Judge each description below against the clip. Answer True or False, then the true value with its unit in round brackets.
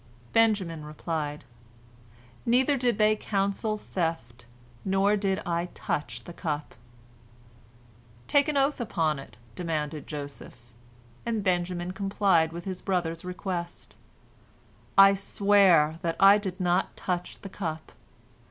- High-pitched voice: False (180 Hz)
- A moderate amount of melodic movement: True (3.7 semitones)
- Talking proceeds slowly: True (115 wpm)